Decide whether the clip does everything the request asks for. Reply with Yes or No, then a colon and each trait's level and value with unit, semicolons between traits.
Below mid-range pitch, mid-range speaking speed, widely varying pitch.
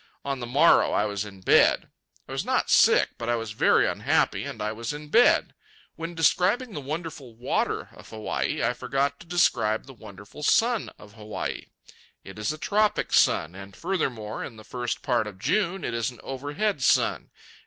Yes: low, 125 Hz; average, 185 wpm; wide, 7.2 semitones